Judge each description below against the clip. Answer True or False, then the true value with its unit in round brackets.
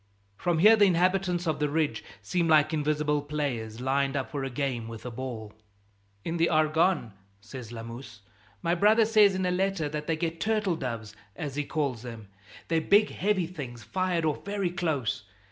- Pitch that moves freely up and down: True (6.0 semitones)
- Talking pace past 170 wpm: True (180 wpm)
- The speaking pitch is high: False (150 Hz)